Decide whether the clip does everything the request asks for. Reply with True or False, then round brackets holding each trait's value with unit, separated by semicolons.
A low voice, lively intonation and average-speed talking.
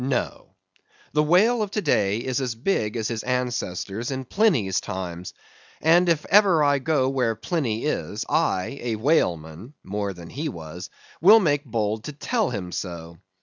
True (125 Hz; 7.6 semitones; 165 wpm)